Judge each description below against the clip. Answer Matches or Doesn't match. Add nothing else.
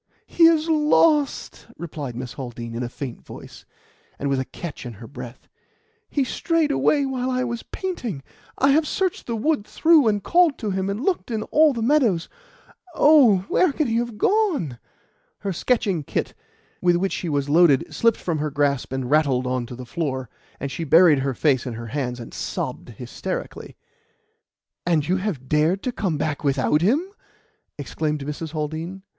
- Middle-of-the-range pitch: Matches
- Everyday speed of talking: Matches